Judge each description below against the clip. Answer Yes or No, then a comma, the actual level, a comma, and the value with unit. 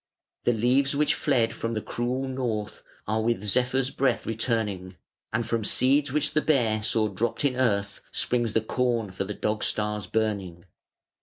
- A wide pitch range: No, average, 3.4 semitones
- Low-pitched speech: Yes, low, 115 Hz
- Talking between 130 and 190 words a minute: Yes, average, 165 wpm